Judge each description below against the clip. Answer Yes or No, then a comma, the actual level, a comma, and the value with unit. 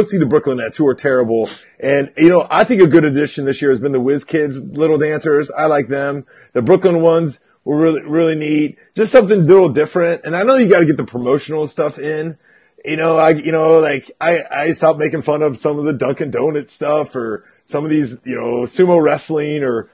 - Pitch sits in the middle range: Yes, medium, 150 Hz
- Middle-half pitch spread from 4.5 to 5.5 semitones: No, narrow, 2.5 semitones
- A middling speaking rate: No, fast, 230 wpm